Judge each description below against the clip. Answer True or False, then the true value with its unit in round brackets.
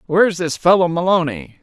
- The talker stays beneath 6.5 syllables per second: True (5.6 syllables/s)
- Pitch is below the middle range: False (170 Hz)